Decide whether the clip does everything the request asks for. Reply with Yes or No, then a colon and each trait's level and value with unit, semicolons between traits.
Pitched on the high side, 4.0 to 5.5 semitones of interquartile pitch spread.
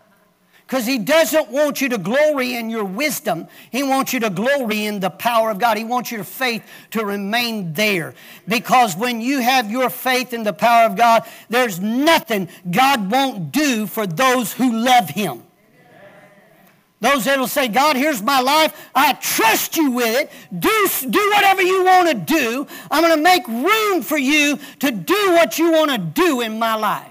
Yes: very high, 255 Hz; average, 5.1 semitones